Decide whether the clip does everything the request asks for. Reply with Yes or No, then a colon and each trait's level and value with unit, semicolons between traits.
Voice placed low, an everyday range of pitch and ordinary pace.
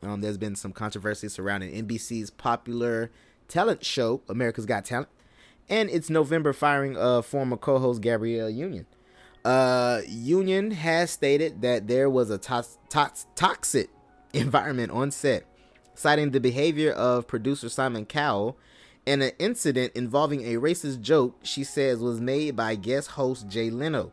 Yes: low, 125 Hz; average, 3.9 semitones; average, 150 wpm